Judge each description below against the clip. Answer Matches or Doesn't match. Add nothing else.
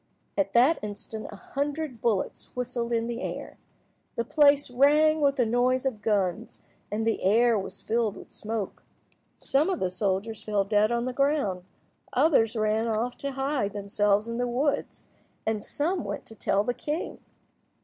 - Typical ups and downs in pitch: Matches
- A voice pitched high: Matches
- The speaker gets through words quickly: Doesn't match